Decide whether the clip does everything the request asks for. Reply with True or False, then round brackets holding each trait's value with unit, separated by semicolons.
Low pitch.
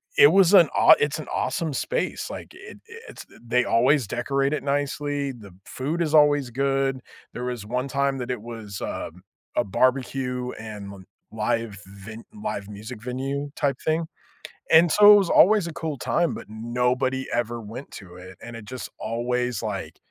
True (130 Hz)